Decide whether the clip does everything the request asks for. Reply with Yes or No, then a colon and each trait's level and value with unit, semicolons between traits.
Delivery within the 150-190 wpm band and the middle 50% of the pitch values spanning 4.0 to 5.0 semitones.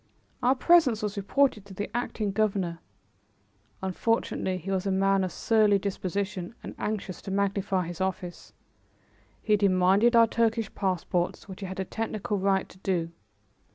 No: average, 155 wpm; narrow, 2.4 semitones